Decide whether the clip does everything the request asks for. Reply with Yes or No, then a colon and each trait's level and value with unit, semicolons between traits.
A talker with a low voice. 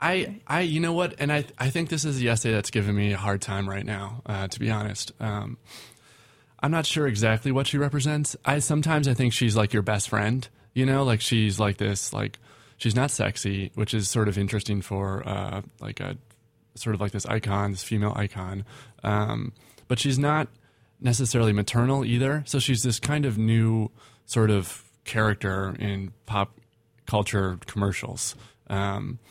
Yes: low, 115 Hz